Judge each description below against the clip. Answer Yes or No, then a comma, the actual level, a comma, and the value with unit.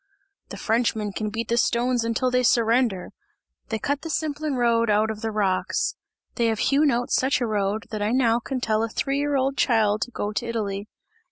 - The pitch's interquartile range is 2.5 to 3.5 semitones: Yes, average, 2.9 semitones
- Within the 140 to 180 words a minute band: No, fast, 205 wpm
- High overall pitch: Yes, high, 230 Hz